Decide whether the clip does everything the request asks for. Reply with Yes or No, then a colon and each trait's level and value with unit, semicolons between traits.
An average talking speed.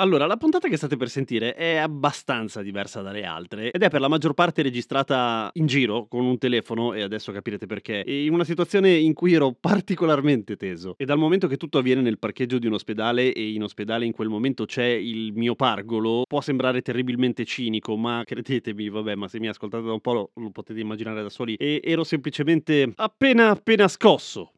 No: fast, 205 wpm